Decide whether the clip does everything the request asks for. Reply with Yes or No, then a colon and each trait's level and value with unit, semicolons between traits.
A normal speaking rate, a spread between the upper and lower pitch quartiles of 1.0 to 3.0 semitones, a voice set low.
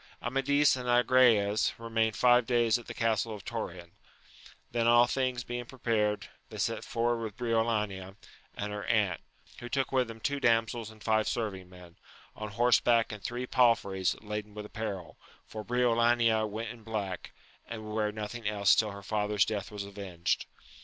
Yes: average, 170 wpm; narrow, 2.5 semitones; low, 110 Hz